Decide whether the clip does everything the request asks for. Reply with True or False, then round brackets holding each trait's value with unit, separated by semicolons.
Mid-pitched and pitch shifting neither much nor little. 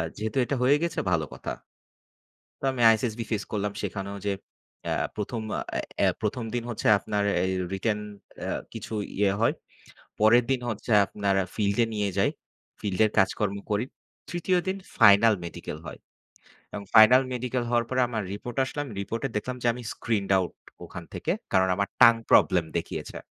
False (110 Hz; 3.2 semitones)